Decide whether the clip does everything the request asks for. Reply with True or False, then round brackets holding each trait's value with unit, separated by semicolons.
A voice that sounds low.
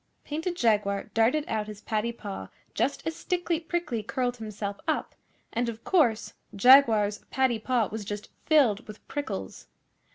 False (230 Hz)